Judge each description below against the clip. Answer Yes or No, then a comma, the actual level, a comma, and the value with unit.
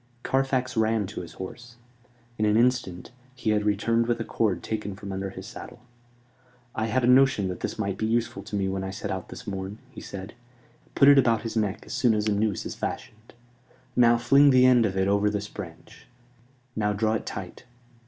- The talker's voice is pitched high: No, low, 110 Hz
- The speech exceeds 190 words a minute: Yes, fast, 205 wpm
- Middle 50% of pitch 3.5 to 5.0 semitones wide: No, average, 3.1 semitones